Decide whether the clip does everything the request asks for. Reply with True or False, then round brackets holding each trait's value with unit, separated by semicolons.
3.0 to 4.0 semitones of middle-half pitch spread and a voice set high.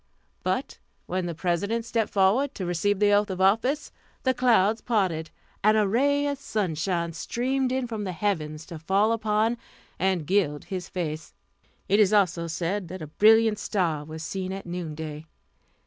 False (4.6 semitones; 195 Hz)